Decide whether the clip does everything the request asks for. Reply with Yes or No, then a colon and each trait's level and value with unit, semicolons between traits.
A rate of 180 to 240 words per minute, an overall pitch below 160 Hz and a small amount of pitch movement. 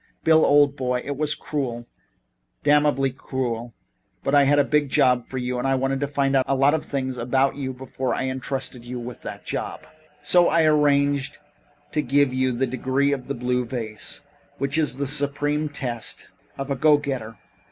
Yes: average, 190 wpm; low, 135 Hz; narrow, 2.2 semitones